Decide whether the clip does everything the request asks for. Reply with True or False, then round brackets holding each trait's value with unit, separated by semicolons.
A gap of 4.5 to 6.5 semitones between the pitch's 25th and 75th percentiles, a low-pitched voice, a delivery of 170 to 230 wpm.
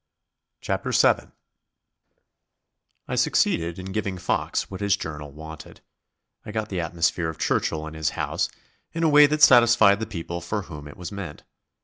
False (5.1 semitones; 90 Hz; 160 wpm)